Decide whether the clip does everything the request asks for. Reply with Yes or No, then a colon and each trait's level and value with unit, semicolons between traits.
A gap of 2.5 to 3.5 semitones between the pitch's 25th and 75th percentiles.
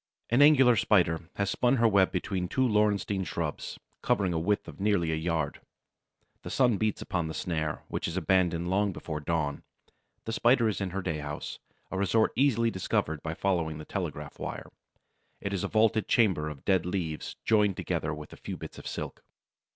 No: average, 4.7 semitones